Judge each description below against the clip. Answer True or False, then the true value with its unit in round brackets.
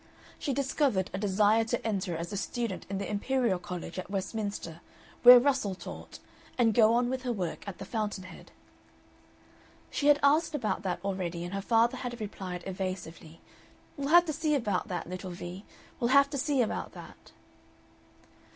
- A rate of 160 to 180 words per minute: True (175 wpm)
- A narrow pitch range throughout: False (5.2 semitones)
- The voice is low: False (210 Hz)